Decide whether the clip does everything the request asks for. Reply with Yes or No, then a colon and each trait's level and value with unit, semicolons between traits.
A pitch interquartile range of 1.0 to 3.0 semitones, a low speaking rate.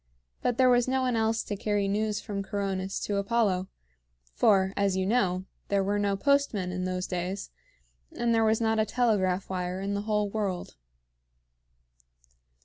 No: average, 2.7 semitones; average, 165 wpm